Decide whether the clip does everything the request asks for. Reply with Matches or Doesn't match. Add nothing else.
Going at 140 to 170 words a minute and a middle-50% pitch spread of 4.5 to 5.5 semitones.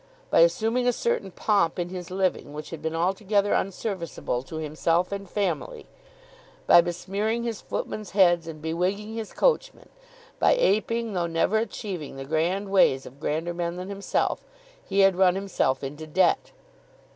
Doesn't match